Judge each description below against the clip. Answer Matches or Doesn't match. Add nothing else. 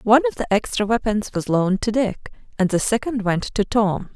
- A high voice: Matches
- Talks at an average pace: Doesn't match